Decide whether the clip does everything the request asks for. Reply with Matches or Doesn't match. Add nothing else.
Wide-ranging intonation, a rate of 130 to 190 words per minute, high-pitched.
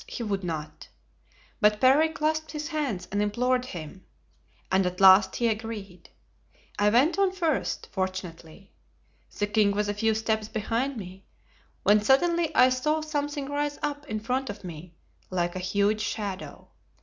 Matches